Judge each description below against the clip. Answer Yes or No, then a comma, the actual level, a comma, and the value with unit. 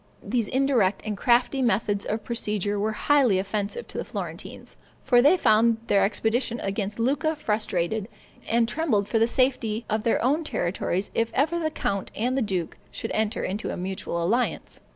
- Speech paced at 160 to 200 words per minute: Yes, average, 175 wpm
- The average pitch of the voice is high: Yes, high, 225 Hz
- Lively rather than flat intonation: No, average, 3.9 semitones